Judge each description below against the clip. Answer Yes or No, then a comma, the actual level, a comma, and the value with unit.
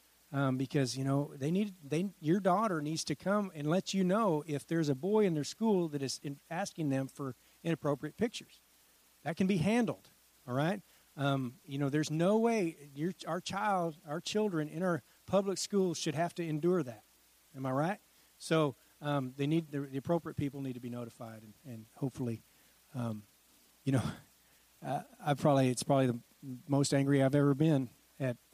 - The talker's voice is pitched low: No, medium, 150 Hz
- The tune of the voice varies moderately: Yes, average, 4.2 semitones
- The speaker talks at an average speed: Yes, average, 190 wpm